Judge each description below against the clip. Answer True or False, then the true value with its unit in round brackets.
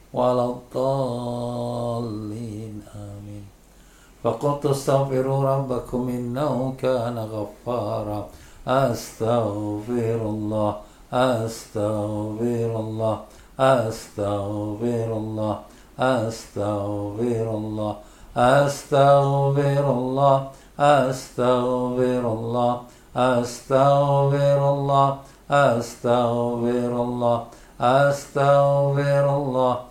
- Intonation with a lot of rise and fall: False (3.6 semitones)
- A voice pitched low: True (120 Hz)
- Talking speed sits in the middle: False (55 wpm)